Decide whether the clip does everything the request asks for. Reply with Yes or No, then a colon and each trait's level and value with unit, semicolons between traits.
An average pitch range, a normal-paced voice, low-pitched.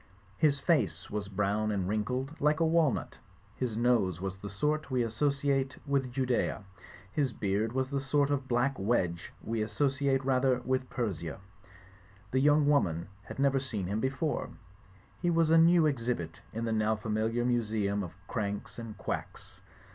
Yes: average, 4.7 semitones; average, 170 wpm; low, 125 Hz